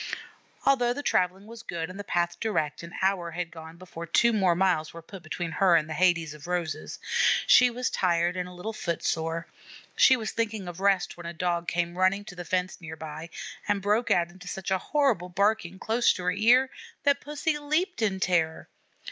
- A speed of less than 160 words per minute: No, fast, 205 wpm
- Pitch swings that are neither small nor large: Yes, average, 4.1 semitones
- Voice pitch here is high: No, medium, 180 Hz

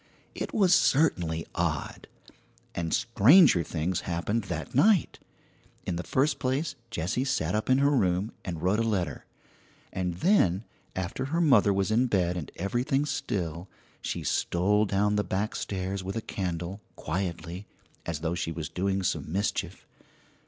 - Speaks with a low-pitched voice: Yes, very low, 95 Hz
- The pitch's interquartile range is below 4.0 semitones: No, average, 5.1 semitones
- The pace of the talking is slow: No, average, 150 wpm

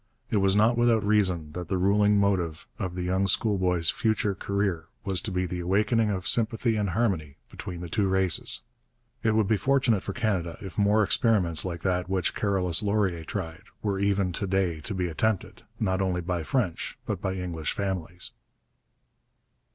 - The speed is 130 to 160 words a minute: No, average, 175 wpm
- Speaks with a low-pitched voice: Yes, very low, 95 Hz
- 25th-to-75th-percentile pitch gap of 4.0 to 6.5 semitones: No, average, 2.8 semitones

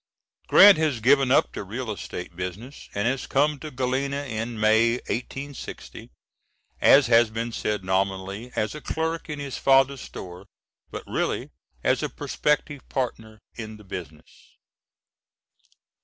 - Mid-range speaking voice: No, low, 120 Hz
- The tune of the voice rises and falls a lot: No, average, 4.5 semitones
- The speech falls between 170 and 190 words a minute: No, average, 140 wpm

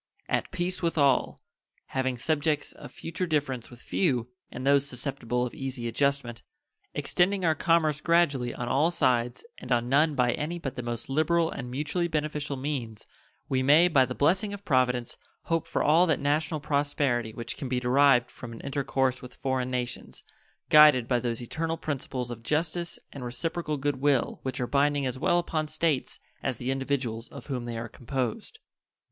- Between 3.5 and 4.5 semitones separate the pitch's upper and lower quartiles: Yes, average, 3.9 semitones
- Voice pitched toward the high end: No, medium, 140 Hz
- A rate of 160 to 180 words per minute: Yes, average, 175 wpm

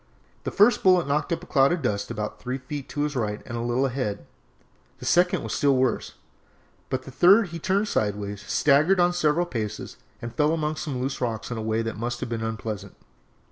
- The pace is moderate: No, fast, 220 wpm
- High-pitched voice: No, low, 130 Hz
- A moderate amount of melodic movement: No, wide, 5.9 semitones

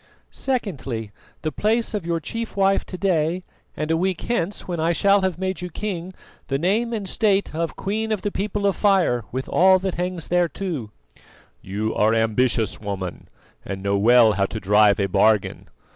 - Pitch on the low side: No, medium, 170 Hz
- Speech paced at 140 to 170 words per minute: No, average, 180 wpm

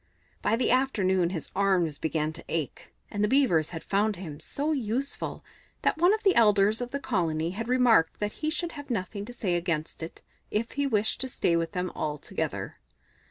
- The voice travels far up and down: Yes, wide, 6.9 semitones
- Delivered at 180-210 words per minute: Yes, average, 195 wpm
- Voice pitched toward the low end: No, high, 205 Hz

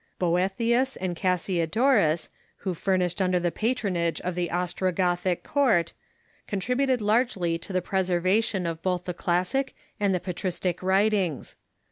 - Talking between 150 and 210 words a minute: No, slow, 135 wpm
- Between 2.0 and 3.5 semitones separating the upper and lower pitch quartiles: Yes, average, 2.9 semitones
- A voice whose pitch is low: No, medium, 185 Hz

